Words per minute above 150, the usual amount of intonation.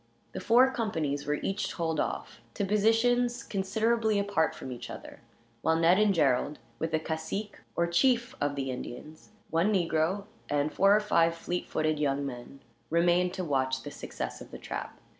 No: average, 175 wpm; wide, 5.8 semitones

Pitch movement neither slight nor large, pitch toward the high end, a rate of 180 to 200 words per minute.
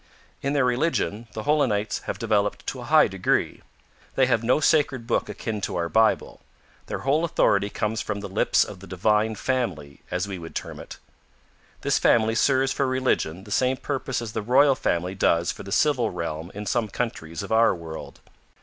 No: average, 5.0 semitones; low, 110 Hz; average, 190 wpm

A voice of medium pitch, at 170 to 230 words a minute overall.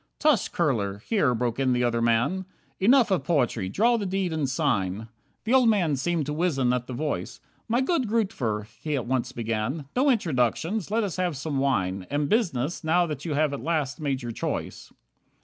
Yes: medium, 145 Hz; average, 200 wpm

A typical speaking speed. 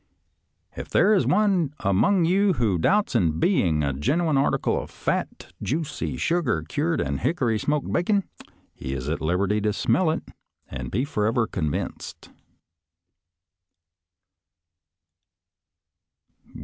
No: slow, 125 wpm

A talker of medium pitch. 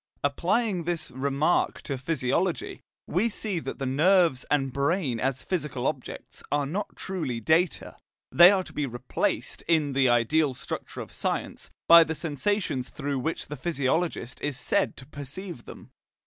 Yes: medium, 150 Hz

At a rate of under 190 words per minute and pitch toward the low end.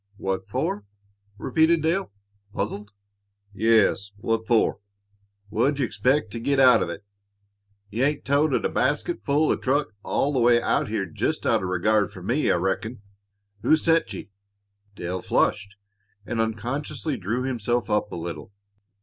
Yes: average, 155 wpm; low, 115 Hz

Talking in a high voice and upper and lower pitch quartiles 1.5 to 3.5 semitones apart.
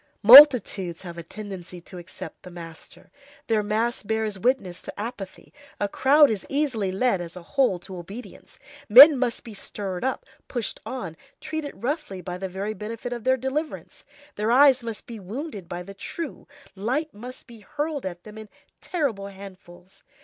No: high, 215 Hz; wide, 5.4 semitones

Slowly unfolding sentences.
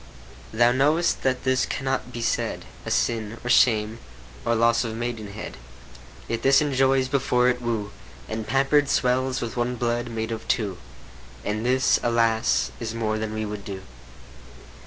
No: average, 155 wpm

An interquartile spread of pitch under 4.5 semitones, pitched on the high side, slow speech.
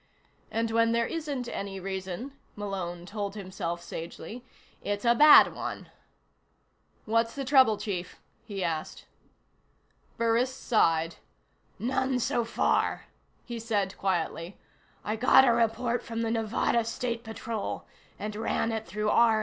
Yes: average, 3.3 semitones; high, 225 Hz; slow, 130 wpm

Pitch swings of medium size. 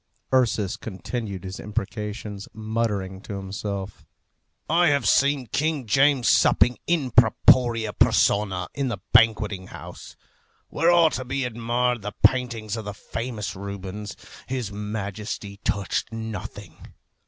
Yes: average, 3.6 semitones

